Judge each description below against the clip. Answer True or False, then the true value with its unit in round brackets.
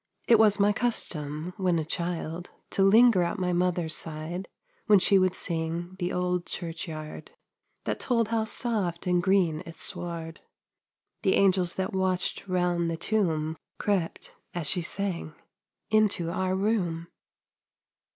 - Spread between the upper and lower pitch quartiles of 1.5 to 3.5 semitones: True (2.8 semitones)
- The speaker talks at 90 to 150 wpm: True (140 wpm)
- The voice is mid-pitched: True (180 Hz)